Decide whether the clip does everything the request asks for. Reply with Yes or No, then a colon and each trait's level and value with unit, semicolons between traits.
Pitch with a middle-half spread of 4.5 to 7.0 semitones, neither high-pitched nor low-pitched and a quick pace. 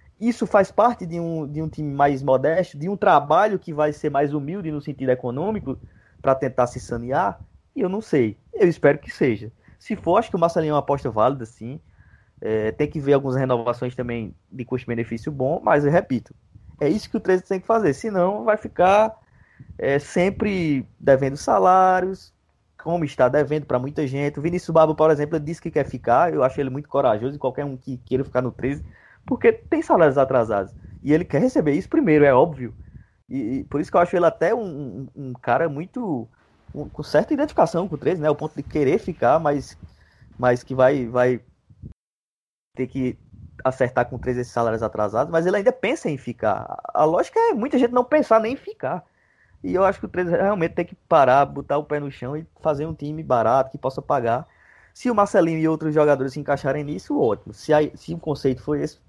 Yes: average, 5.2 semitones; medium, 145 Hz; fast, 210 wpm